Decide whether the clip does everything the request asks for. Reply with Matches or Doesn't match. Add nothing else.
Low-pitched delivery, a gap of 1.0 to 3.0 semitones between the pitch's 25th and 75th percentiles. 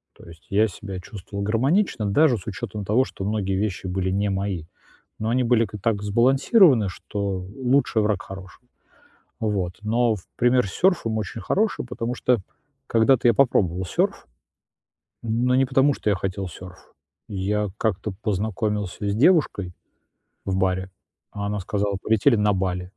Doesn't match